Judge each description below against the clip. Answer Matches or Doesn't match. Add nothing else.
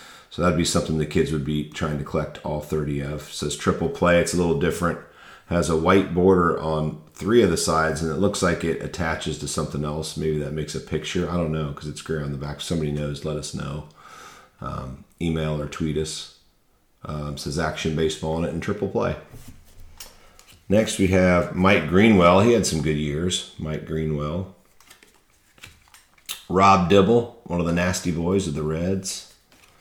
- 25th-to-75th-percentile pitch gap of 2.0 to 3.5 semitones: Matches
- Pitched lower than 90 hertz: Matches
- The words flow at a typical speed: Matches